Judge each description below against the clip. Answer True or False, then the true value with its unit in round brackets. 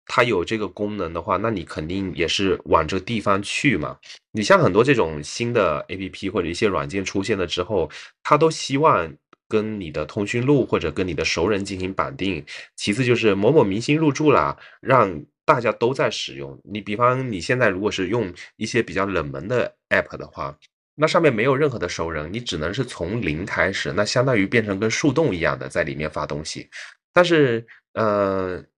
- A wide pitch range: False (5.0 semitones)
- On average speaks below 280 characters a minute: False (295 characters per minute)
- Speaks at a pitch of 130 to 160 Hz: False (105 Hz)